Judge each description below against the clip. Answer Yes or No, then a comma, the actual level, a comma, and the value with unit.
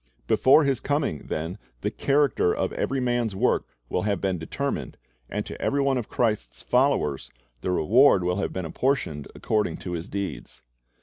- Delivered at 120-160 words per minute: No, average, 175 wpm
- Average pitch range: No, wide, 7.3 semitones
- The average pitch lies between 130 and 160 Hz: No, low, 100 Hz